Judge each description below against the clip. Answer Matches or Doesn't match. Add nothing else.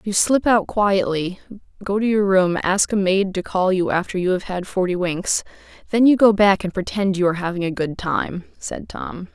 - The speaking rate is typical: Doesn't match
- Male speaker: Doesn't match